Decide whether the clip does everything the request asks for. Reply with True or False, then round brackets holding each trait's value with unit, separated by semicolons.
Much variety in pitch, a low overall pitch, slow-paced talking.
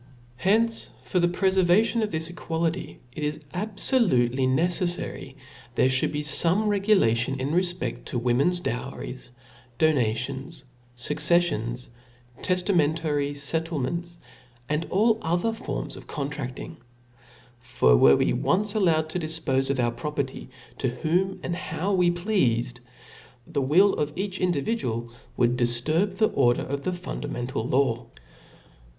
False (5.7 semitones; 155 Hz; 130 wpm)